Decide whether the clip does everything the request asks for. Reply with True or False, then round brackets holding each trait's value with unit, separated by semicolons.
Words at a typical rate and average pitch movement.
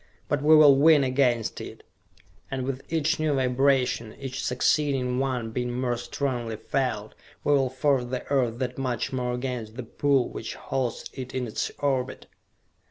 False (165 wpm; 2.0 semitones)